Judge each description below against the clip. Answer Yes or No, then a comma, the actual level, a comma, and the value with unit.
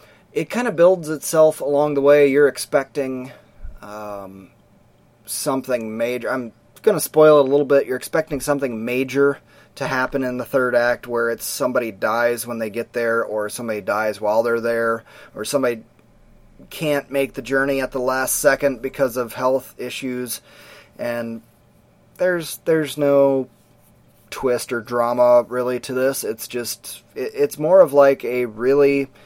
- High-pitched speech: No, low, 130 Hz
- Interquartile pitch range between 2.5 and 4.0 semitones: Yes, average, 3.2 semitones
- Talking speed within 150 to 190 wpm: Yes, average, 160 wpm